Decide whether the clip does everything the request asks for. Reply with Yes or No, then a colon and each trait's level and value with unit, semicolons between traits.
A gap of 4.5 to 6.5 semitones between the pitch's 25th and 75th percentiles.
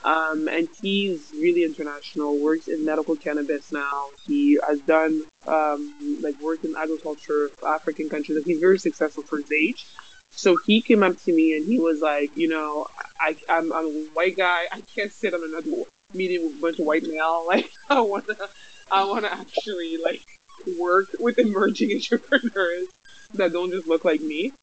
Yes: average, 5.0 semitones